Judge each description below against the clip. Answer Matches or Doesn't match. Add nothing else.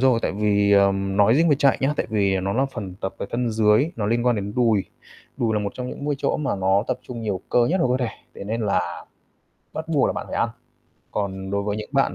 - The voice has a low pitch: Matches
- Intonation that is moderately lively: Matches